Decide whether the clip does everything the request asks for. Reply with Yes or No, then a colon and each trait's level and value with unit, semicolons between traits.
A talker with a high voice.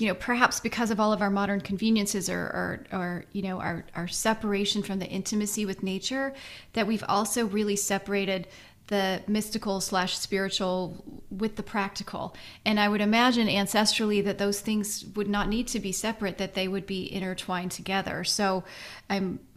Yes: high, 200 Hz